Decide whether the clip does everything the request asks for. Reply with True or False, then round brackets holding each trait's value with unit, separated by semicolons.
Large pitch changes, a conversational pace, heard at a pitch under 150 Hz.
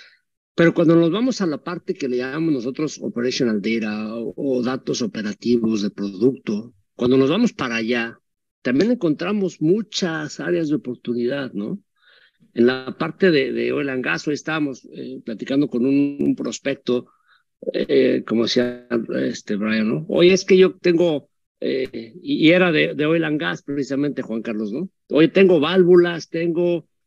True (6.1 semitones; 165 wpm; 140 Hz)